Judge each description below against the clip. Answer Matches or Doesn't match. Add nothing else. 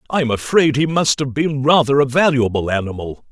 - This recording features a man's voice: Matches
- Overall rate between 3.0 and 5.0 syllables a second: Doesn't match